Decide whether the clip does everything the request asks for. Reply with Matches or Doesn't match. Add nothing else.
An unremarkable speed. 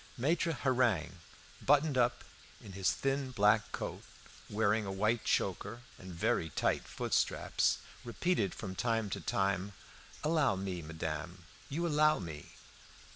Doesn't match